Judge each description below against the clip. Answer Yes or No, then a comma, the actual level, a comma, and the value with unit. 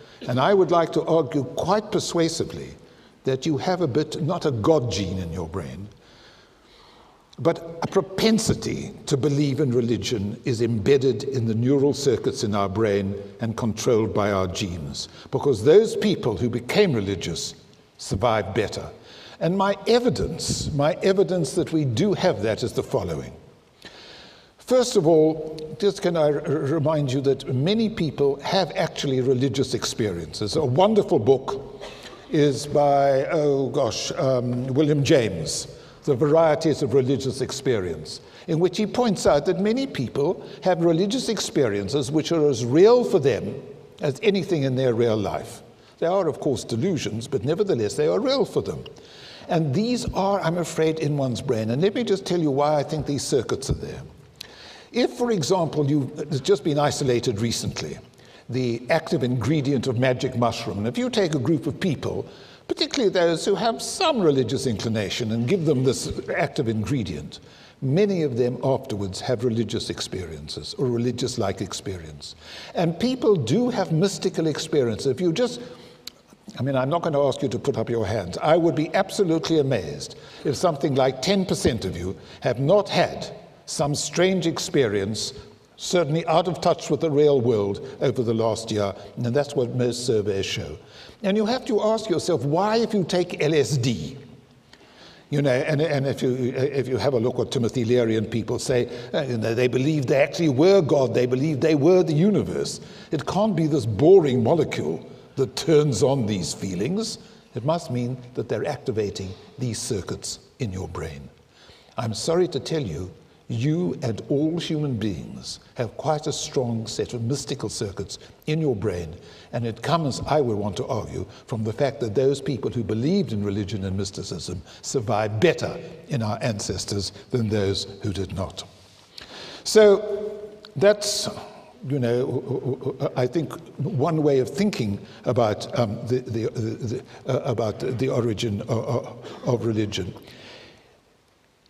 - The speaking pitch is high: No, medium, 140 Hz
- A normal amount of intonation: No, wide, 6.1 semitones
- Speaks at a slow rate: No, average, 165 wpm